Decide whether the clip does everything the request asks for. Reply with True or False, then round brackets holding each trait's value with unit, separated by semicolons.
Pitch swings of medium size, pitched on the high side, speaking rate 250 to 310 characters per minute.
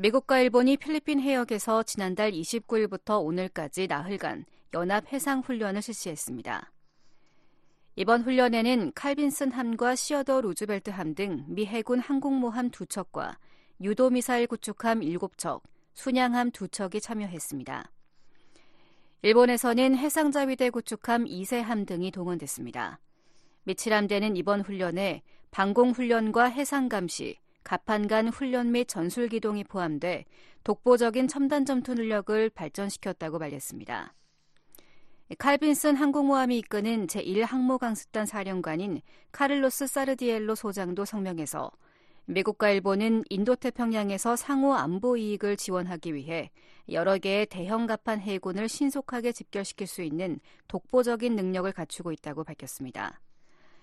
True (4.5 semitones; 220 Hz; 305 characters per minute)